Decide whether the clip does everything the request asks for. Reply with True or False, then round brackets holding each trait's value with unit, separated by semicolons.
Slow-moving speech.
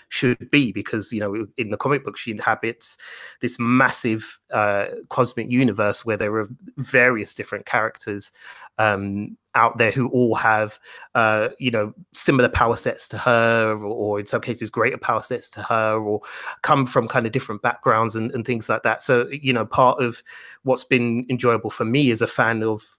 False (190 wpm)